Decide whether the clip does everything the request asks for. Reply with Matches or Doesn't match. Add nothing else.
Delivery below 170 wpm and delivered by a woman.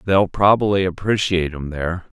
Doesn't match